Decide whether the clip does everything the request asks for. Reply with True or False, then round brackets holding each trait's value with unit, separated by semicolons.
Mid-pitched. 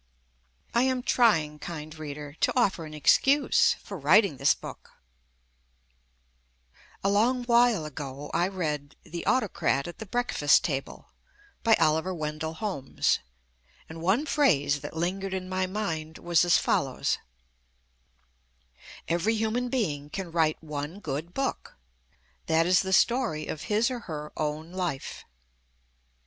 True (170 Hz)